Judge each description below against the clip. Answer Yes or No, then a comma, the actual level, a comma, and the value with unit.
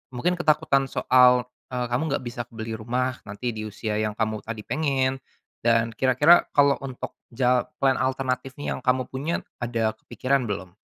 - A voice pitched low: Yes, low, 125 Hz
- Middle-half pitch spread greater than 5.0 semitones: No, average, 2.8 semitones